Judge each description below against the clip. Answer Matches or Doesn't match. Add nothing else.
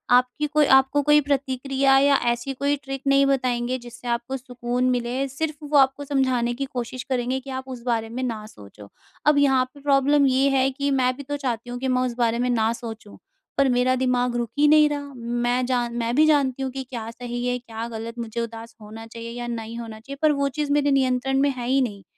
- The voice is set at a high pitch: Matches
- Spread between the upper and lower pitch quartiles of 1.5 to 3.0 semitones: Matches